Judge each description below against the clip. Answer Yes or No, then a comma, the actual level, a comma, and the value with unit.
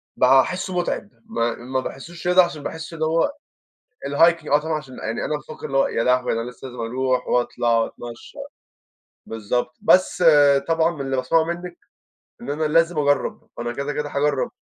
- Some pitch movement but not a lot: Yes, average, 4.7 semitones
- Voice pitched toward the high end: No, medium, 145 Hz